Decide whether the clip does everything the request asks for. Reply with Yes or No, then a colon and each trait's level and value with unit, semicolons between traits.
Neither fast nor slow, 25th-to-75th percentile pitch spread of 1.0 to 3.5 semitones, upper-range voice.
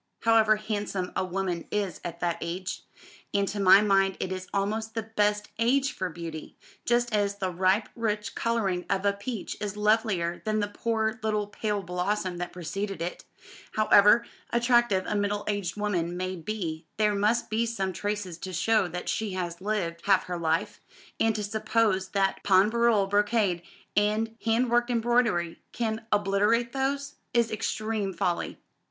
Yes: average, 165 wpm; average, 3.0 semitones; high, 205 Hz